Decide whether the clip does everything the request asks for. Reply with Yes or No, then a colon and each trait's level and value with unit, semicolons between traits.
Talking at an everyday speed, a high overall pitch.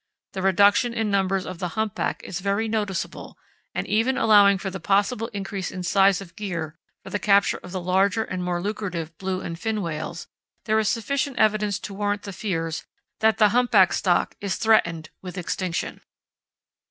Yes: average, 175 wpm; high, 195 Hz